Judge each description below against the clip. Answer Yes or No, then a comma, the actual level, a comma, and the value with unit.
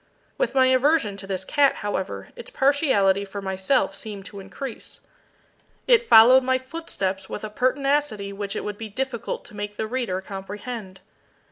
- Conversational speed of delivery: Yes, average, 160 wpm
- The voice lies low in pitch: No, high, 215 Hz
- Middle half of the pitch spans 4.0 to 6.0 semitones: Yes, average, 5.0 semitones